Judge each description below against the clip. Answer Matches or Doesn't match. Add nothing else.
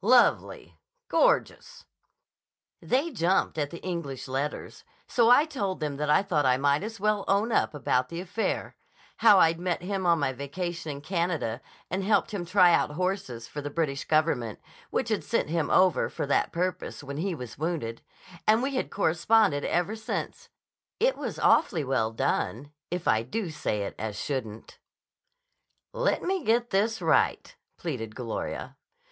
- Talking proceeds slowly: Doesn't match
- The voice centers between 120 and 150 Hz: Doesn't match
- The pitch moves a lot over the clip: Matches